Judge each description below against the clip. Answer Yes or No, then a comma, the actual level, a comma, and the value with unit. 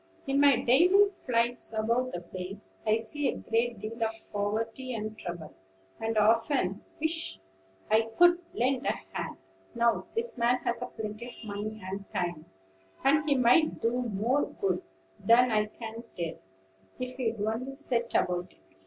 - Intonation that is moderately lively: Yes, average, 3.2 semitones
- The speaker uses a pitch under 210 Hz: No, high, 230 Hz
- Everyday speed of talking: Yes, average, 155 wpm